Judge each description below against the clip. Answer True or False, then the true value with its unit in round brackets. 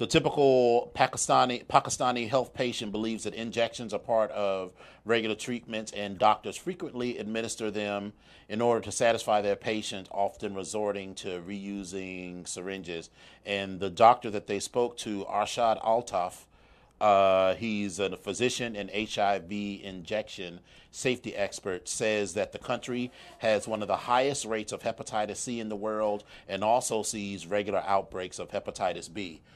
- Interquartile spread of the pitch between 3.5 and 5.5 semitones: False (2.8 semitones)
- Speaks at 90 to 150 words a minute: True (145 wpm)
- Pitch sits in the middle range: False (105 Hz)